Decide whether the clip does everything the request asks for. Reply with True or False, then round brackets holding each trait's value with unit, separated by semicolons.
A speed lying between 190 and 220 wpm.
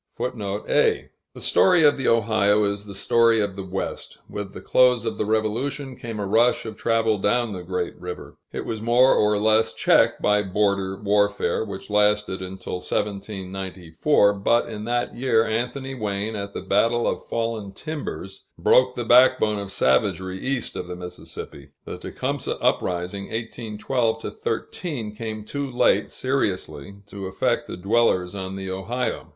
False (155 wpm)